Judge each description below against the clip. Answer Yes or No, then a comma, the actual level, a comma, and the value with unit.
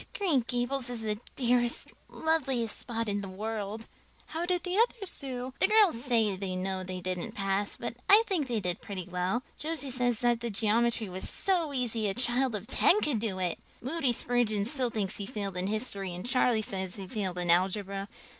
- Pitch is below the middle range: No, high, 225 Hz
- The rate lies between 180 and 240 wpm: Yes, average, 190 wpm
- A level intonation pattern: No, average, 4.7 semitones